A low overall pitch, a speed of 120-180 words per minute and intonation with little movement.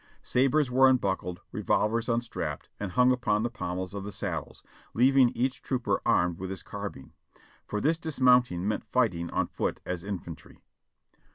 No: low, 115 Hz; average, 155 wpm; average, 5.1 semitones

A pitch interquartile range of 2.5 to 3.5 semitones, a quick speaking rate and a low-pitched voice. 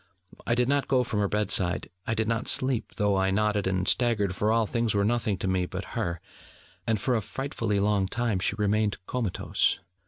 Yes: average, 3.0 semitones; fast, 210 wpm; low, 105 Hz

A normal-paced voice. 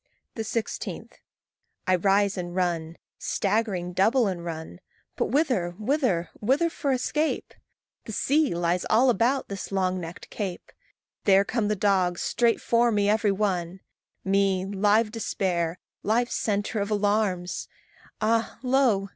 No: slow, 130 wpm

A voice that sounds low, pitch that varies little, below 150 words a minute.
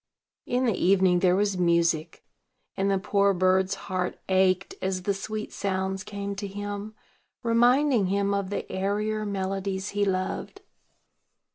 No: high, 195 Hz; narrow, 1.5 semitones; average, 140 wpm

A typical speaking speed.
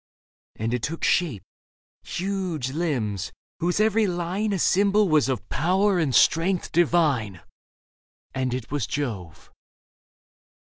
No: slow, 125 wpm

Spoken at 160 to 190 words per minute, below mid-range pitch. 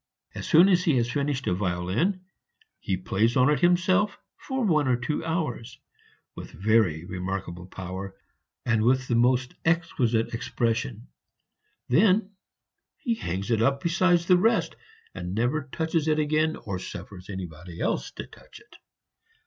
No: average, 150 wpm; low, 125 Hz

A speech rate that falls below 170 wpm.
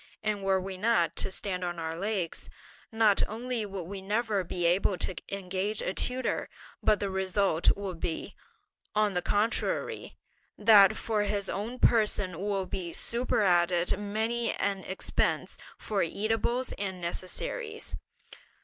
Yes: average, 140 wpm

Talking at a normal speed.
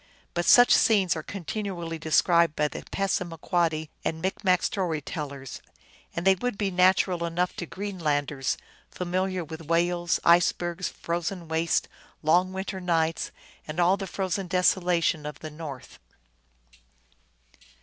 No: slow, 130 wpm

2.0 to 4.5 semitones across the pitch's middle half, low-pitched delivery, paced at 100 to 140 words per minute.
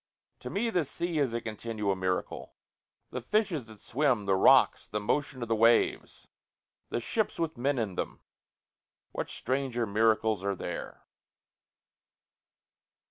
No: average, 5.1 semitones; low, 115 Hz; slow, 135 wpm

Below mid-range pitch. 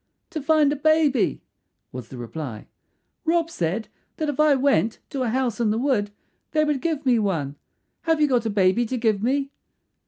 No: very high, 255 Hz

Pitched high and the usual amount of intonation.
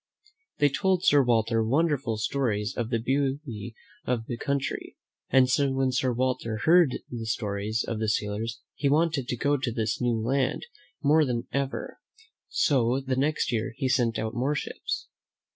No: low, 125 Hz; average, 3.6 semitones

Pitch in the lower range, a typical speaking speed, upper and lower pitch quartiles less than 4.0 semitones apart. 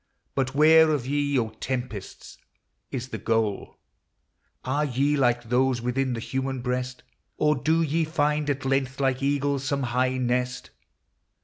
Yes: low, 130 Hz; average, 145 wpm; narrow, 2.4 semitones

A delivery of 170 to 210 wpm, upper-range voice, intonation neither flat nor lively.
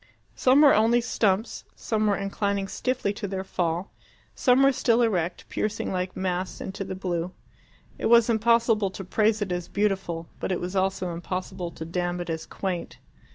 Yes: average, 175 wpm; high, 195 Hz; average, 3.4 semitones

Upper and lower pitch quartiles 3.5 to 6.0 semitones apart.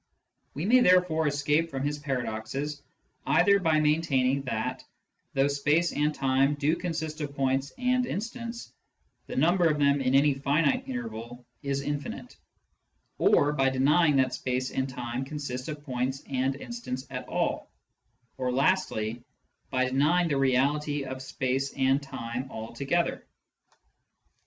No: average, 2.7 semitones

